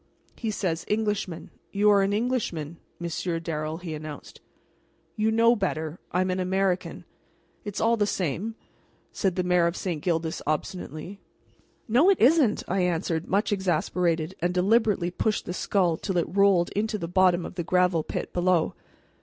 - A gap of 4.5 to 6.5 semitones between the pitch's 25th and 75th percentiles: No, average, 3.5 semitones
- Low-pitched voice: No, medium, 185 Hz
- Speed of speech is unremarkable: Yes, average, 170 wpm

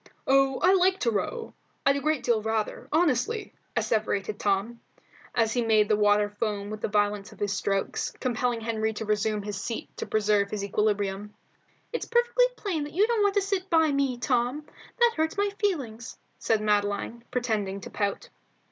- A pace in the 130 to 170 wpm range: No, average, 180 wpm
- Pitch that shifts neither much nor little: No, wide, 6.9 semitones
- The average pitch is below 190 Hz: No, high, 225 Hz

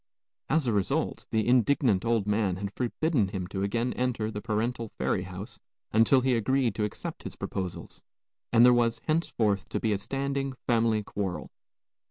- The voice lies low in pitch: Yes, low, 115 Hz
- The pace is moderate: Yes, average, 170 wpm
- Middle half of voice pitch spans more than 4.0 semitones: No, average, 3.6 semitones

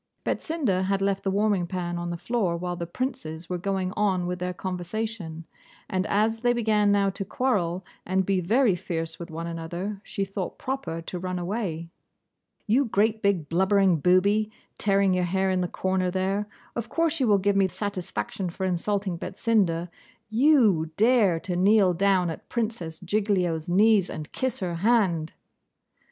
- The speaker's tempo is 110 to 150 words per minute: No, average, 170 wpm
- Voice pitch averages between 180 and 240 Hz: Yes, high, 190 Hz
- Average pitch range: Yes, average, 3.2 semitones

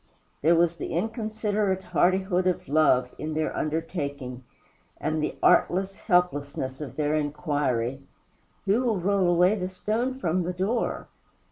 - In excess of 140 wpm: No, slow, 135 wpm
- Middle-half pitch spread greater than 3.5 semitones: Yes, average, 4.3 semitones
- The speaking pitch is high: No, medium, 175 Hz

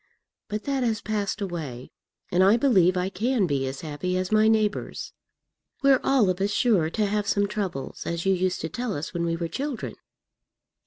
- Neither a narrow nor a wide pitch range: Yes, average, 4.2 semitones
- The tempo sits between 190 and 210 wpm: Yes, average, 195 wpm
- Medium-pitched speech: No, high, 195 Hz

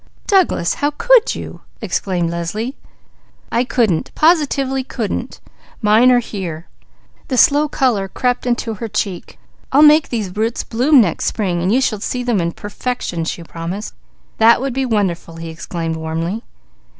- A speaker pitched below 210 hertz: No, high, 220 Hz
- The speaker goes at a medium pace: Yes, average, 150 wpm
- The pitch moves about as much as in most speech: No, wide, 6.7 semitones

